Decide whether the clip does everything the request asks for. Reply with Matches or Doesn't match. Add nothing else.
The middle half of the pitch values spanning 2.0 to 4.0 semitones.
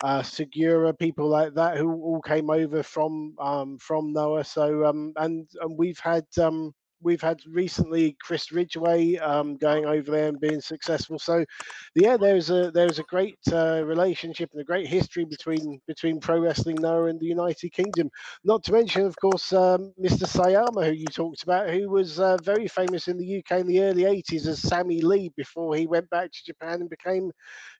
Matches